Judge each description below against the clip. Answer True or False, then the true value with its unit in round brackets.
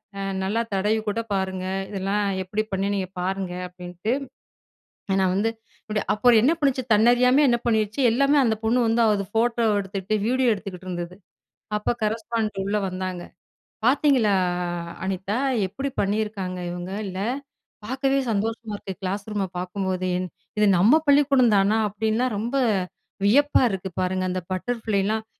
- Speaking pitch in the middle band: False (210 Hz)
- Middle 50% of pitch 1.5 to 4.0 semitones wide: True (3.4 semitones)